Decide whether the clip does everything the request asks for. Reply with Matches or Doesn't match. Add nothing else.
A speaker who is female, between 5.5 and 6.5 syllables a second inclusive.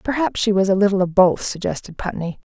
Matches